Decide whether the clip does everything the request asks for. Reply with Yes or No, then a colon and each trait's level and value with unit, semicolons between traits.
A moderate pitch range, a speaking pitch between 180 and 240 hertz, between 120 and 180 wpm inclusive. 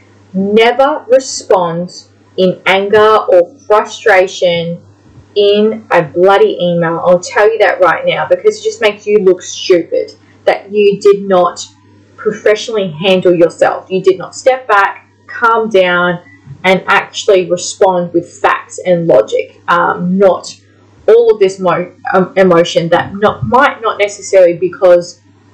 Yes: average, 3.2 semitones; high, 190 Hz; slow, 135 wpm